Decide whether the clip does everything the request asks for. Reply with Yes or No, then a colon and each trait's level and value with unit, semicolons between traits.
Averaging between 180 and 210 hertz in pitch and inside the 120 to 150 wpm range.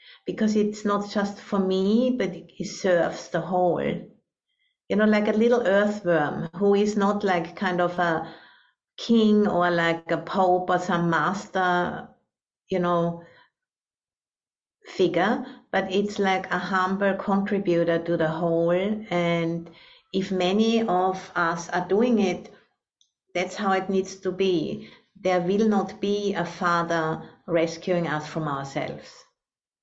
Yes: medium, 185 Hz; slow, 135 wpm